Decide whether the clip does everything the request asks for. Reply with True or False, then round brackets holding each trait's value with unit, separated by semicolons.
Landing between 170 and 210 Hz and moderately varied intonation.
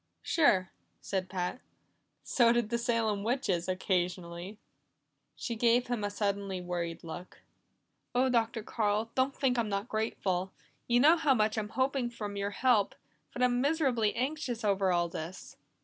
False (220 Hz; 4.3 semitones)